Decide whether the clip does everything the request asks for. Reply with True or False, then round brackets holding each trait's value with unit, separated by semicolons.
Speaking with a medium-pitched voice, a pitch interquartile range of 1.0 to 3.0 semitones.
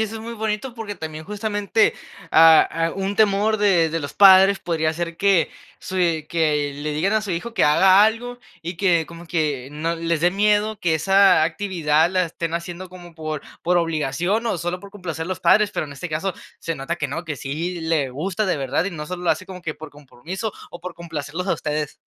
False (175 Hz; 3.8 semitones)